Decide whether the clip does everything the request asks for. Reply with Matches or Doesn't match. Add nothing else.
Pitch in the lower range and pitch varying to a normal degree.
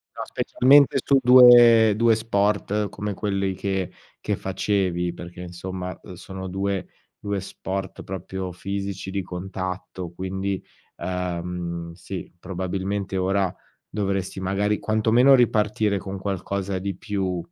Doesn't match